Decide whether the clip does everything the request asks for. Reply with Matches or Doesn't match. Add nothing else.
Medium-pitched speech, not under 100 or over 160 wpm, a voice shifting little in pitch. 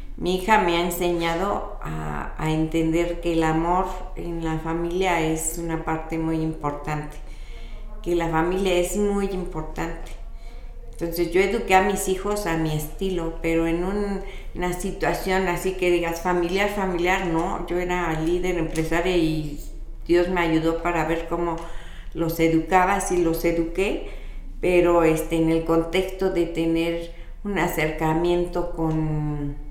Matches